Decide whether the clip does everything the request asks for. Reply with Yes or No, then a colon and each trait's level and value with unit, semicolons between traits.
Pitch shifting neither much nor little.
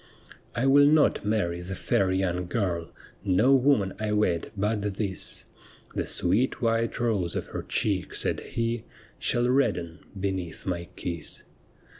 Yes: average, 4.5 semitones